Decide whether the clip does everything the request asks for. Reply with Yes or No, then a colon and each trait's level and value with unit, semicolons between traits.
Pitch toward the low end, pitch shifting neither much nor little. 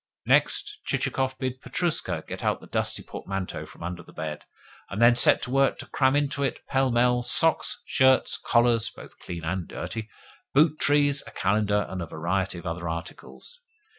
No: low, 120 Hz; wide, 6.5 semitones